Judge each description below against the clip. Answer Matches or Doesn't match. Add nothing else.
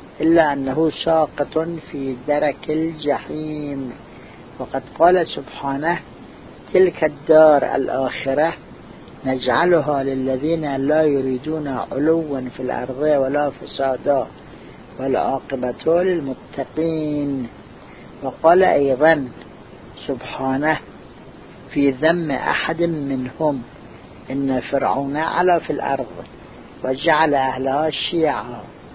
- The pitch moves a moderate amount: Matches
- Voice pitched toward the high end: Doesn't match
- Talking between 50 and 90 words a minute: Matches